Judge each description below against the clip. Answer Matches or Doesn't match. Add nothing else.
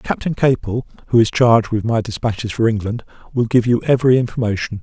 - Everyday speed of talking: Matches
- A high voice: Doesn't match